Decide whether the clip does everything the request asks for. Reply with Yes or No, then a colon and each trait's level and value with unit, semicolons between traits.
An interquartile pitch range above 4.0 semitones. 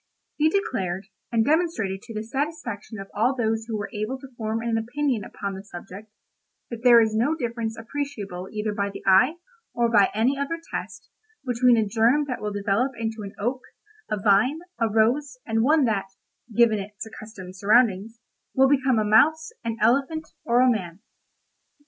No: average, 3.6 semitones